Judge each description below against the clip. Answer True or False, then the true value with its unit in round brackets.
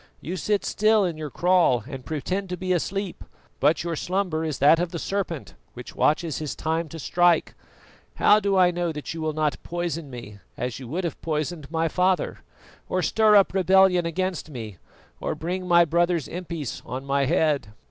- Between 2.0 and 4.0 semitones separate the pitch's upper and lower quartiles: True (3.4 semitones)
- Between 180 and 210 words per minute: True (190 wpm)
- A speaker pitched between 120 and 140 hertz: False (165 Hz)